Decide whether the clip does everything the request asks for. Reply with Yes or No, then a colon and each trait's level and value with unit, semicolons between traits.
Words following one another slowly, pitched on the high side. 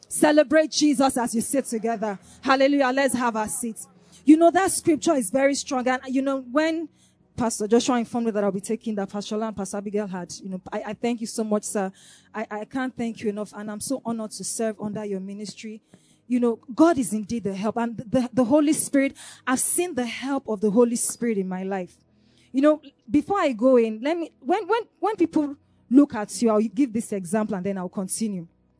No: fast, 220 wpm; high, 230 Hz